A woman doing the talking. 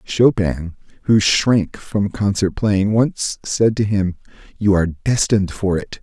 No: male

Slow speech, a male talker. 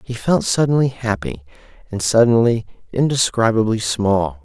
Yes: slow, 110 wpm; male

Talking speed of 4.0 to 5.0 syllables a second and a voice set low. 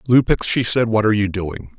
No: 5.6 syllables/s; low, 105 Hz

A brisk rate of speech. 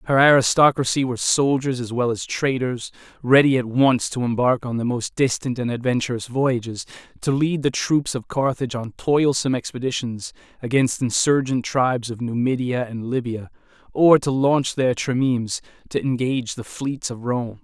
No: average, 160 wpm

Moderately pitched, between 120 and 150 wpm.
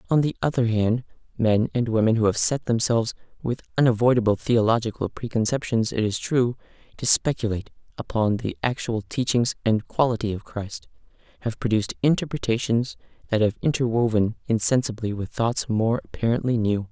No: low, 115 Hz; average, 140 wpm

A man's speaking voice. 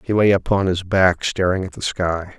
Yes: male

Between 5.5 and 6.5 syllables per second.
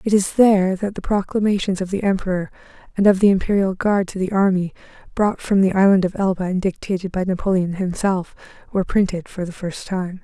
Yes: 5.8 syllables/s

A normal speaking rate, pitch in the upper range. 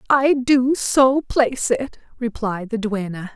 Yes: average, 145 wpm; high, 245 Hz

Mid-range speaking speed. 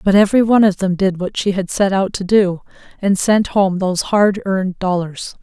No: fast, 220 wpm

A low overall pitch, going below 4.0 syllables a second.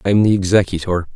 No: very low, 95 Hz; 7.1 syllables/s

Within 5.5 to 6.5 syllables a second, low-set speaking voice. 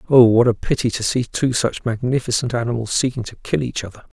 Yes: 6.0 syllables/s; low, 120 Hz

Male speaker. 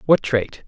Yes: male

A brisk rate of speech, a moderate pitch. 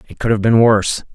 No: fast, 265 wpm; low, 110 Hz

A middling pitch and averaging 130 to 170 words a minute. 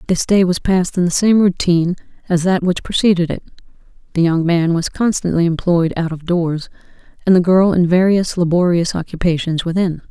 No: medium, 175 Hz; average, 180 wpm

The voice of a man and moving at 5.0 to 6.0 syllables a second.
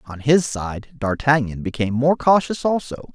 No: male; 4.7 syllables/s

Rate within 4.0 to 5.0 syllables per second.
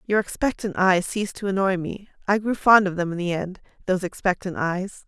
No: 5.6 syllables/s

